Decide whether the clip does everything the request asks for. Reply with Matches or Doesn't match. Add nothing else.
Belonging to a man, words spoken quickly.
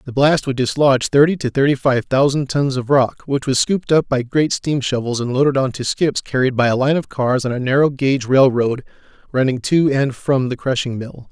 Matches